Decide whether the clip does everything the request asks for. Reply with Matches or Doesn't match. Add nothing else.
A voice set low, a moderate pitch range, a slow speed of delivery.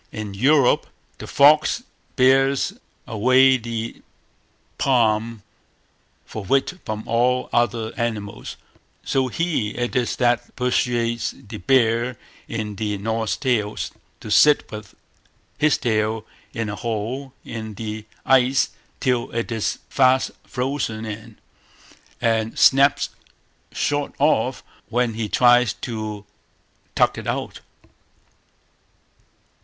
Matches